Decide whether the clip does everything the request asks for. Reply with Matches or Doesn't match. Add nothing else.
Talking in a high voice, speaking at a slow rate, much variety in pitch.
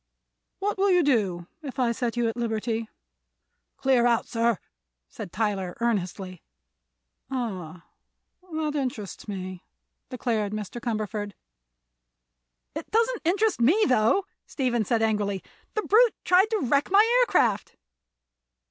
Matches